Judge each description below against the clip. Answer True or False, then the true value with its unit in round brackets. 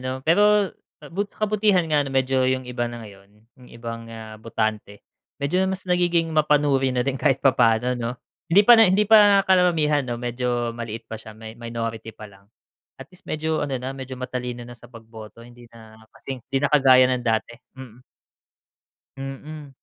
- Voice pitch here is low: True (130 Hz)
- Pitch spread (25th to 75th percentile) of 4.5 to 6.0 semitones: True (5.0 semitones)